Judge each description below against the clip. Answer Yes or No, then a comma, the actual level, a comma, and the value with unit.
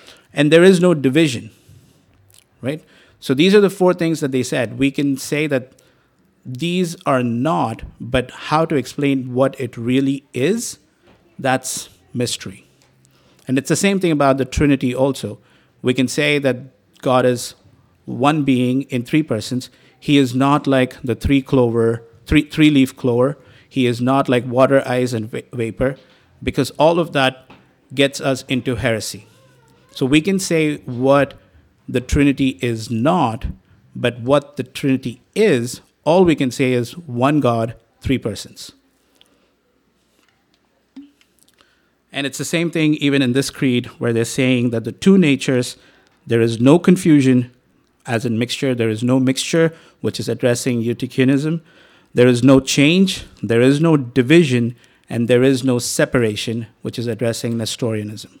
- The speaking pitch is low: Yes, low, 130 Hz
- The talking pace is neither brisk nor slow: Yes, average, 155 wpm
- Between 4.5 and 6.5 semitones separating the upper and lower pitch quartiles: No, average, 3.0 semitones